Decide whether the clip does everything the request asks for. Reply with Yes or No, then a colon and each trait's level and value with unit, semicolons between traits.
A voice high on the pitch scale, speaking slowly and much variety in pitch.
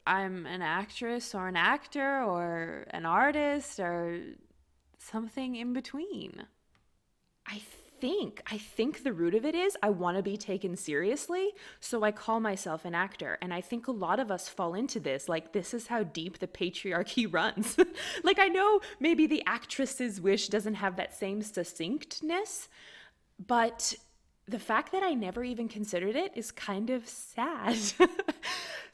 No: high, 225 Hz; average, 160 wpm; wide, 7.0 semitones